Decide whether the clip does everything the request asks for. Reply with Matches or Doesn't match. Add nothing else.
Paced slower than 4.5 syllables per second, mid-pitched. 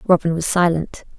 Doesn't match